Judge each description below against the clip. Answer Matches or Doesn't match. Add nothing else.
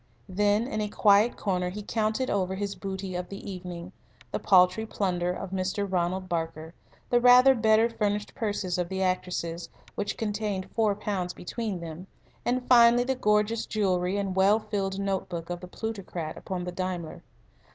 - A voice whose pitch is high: Matches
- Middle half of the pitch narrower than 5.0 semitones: Matches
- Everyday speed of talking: Matches